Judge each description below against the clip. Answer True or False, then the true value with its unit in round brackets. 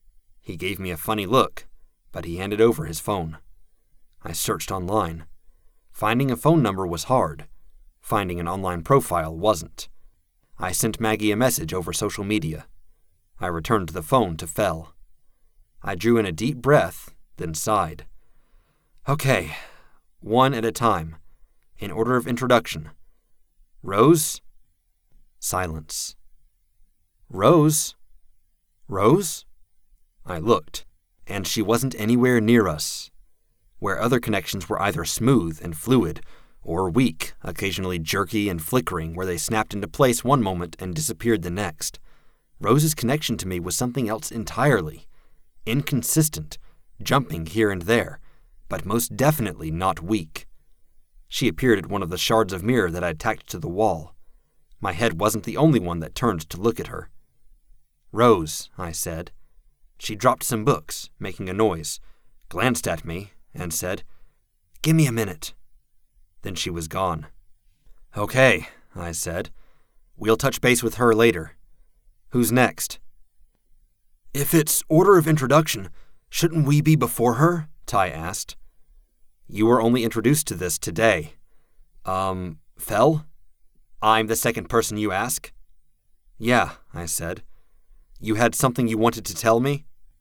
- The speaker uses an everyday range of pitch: False (5.8 semitones)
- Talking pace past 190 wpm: False (140 wpm)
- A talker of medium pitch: False (100 Hz)